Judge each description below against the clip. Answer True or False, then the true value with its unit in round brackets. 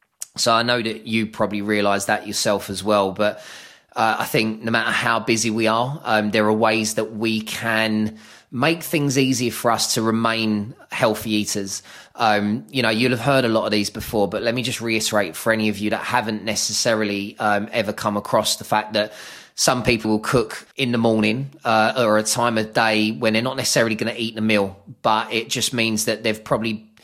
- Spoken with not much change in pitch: True (1.3 semitones)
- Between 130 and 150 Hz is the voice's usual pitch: False (110 Hz)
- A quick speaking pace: True (215 wpm)